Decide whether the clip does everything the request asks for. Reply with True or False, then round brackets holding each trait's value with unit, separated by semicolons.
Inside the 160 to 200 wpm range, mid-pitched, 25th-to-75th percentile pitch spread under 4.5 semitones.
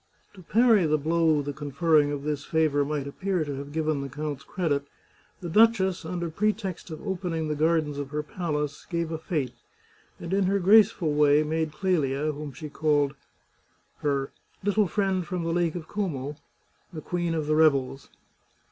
True (175 wpm; 155 Hz; 3.5 semitones)